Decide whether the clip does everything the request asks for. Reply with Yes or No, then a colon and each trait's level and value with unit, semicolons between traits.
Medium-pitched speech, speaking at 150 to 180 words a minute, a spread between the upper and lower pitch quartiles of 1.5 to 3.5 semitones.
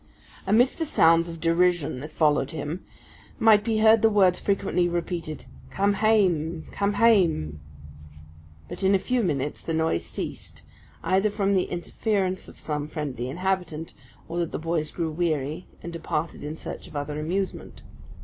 No: medium, 170 Hz; average, 160 wpm; average, 4.2 semitones